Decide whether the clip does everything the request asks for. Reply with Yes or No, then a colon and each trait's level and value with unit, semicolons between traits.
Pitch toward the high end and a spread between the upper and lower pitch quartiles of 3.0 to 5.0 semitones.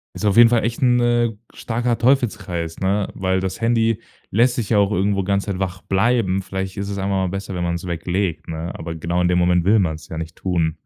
No: very low, 95 Hz; average, 4.2 semitones